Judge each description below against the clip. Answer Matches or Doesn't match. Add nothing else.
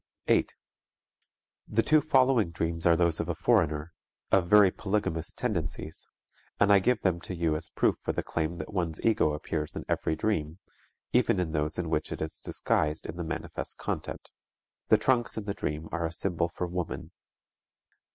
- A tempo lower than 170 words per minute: Doesn't match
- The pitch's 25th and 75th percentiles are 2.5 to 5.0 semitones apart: Matches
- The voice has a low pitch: Matches